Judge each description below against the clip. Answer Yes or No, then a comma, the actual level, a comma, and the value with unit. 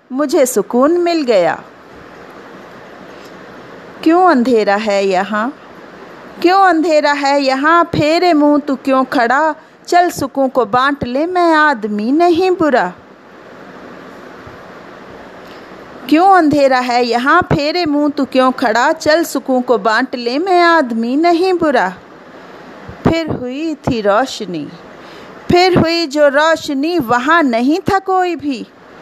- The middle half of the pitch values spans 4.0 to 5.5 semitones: Yes, average, 4.7 semitones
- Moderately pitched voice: No, very high, 290 Hz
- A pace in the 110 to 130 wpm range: Yes, average, 120 wpm